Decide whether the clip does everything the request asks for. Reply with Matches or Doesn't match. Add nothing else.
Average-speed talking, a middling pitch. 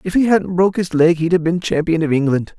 Doesn't match